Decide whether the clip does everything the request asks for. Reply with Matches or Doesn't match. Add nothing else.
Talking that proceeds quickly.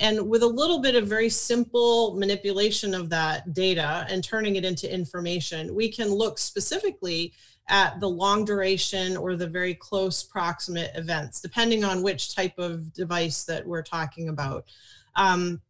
Doesn't match